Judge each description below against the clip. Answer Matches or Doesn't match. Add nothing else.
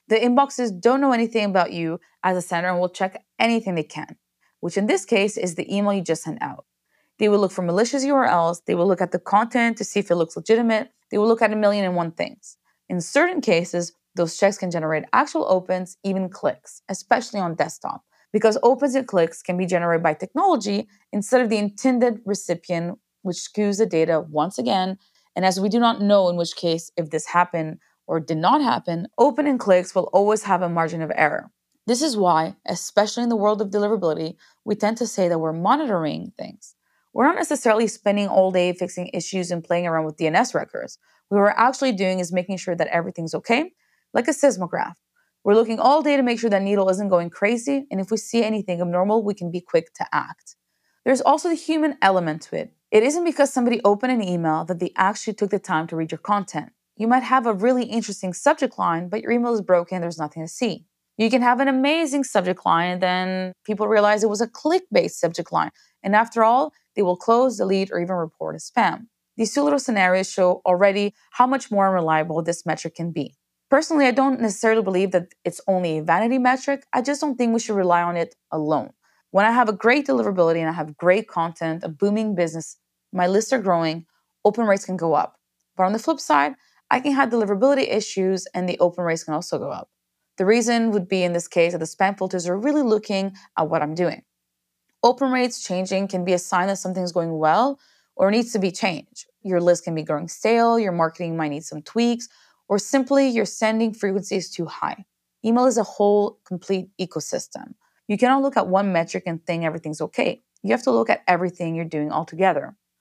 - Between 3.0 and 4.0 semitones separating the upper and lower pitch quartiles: Doesn't match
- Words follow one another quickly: Matches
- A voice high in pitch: Matches